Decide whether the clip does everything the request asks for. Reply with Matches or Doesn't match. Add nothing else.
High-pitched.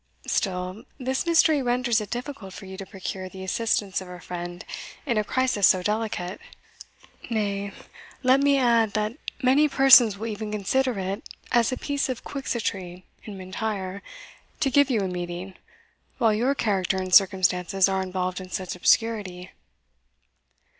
Matches